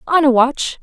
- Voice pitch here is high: Yes, very high, 280 Hz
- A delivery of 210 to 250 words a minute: Yes, fast, 215 wpm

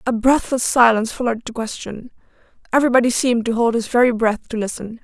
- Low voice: No, high, 235 Hz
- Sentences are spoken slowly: No, average, 165 wpm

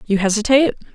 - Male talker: No, female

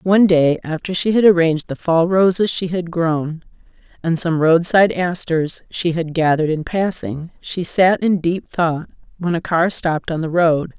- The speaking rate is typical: Yes, average, 185 wpm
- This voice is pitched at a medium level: Yes, medium, 170 Hz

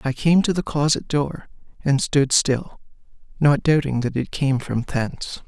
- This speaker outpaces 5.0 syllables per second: No, 4.4 syllables/s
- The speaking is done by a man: Yes, male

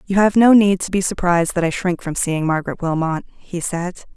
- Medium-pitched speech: Yes, medium, 180 Hz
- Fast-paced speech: Yes, fast, 230 wpm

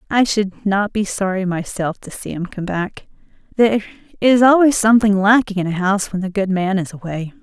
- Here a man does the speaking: No, female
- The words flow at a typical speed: Yes, average, 195 wpm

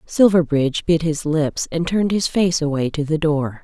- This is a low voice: No, medium, 160 Hz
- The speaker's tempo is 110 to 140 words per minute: No, average, 200 wpm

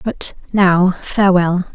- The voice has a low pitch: No, medium, 185 Hz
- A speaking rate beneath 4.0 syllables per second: Yes, 3.5 syllables/s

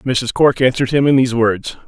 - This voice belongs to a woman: No, male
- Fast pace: Yes, fast, 225 wpm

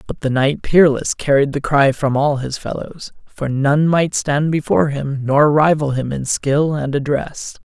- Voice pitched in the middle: Yes, medium, 145 Hz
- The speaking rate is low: No, average, 190 wpm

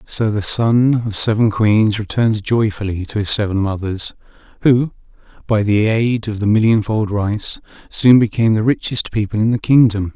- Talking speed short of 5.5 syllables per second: Yes, 4.8 syllables/s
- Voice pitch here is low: Yes, low, 110 Hz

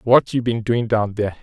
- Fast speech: Yes, fast, 250 wpm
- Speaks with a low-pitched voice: Yes, low, 115 Hz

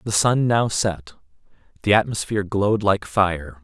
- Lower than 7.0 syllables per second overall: Yes, 4.6 syllables/s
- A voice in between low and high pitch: No, low, 100 Hz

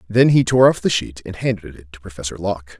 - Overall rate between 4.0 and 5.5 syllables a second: No, 6.2 syllables/s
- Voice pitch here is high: No, low, 100 Hz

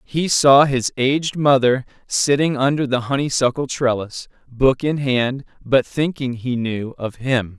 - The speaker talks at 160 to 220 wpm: No, average, 150 wpm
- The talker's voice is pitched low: Yes, low, 130 Hz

